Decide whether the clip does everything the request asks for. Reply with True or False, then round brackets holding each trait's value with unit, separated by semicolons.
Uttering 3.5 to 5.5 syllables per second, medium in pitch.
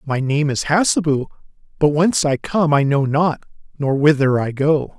True (4.7 syllables/s; 150 Hz)